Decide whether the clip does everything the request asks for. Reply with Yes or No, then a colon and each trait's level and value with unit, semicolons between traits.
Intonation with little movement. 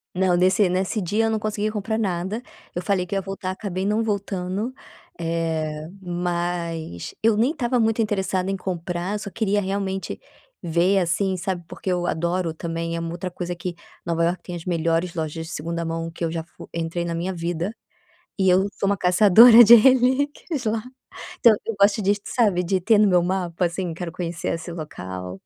No: average, 3.3 semitones